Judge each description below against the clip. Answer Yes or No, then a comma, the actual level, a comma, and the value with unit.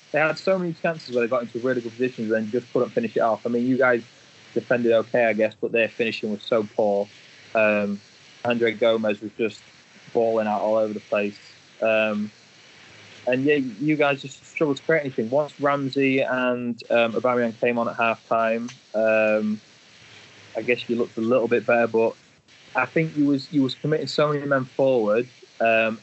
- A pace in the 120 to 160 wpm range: No, average, 195 wpm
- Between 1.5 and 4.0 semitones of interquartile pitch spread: Yes, average, 3.6 semitones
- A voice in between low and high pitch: No, low, 120 Hz